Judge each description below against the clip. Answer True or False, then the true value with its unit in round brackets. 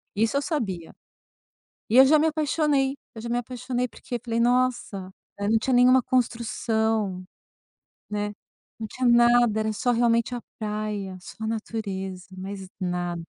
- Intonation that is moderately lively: True (3.2 semitones)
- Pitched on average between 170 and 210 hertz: False (230 Hz)